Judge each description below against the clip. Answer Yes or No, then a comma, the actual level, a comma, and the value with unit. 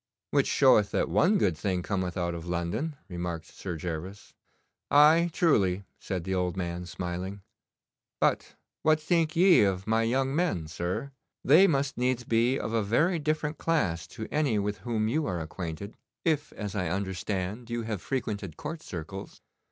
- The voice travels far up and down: Yes, wide, 8.1 semitones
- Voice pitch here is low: Yes, low, 105 Hz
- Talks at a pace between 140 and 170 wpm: Yes, average, 165 wpm